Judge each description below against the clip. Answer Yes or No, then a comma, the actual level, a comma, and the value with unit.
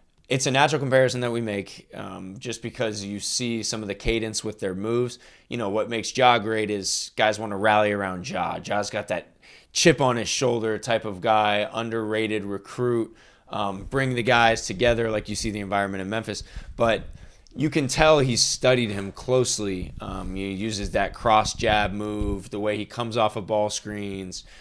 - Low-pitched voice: Yes, low, 110 Hz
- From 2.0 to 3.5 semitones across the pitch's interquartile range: Yes, average, 2.9 semitones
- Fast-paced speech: No, average, 195 wpm